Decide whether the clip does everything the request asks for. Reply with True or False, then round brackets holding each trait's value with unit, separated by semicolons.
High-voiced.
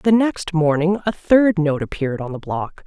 False (170 Hz)